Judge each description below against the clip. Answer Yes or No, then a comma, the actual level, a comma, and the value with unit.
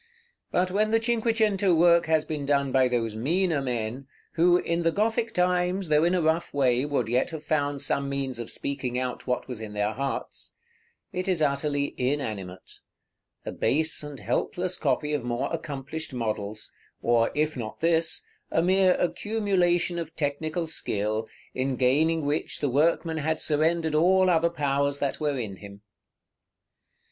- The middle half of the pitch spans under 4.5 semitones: No, average, 4.8 semitones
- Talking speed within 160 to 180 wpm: Yes, average, 165 wpm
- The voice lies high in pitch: No, medium, 150 Hz